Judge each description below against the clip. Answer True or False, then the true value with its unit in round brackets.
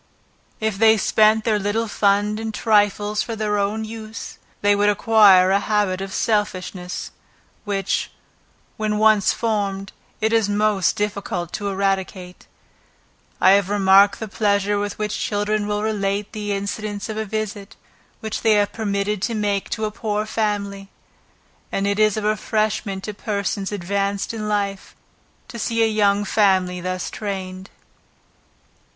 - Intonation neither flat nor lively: False (1.5 semitones)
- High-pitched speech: True (205 Hz)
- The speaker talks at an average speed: True (150 wpm)